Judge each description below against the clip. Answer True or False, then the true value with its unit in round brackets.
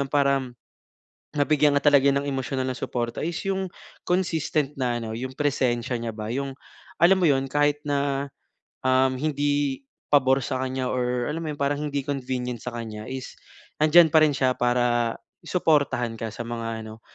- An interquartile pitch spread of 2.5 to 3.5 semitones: True (2.9 semitones)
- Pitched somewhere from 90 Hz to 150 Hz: True (135 Hz)